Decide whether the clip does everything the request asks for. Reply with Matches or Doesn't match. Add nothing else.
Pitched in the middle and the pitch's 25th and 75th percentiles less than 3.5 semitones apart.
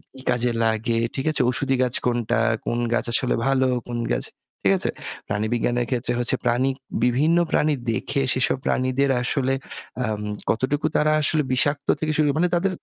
Doesn't match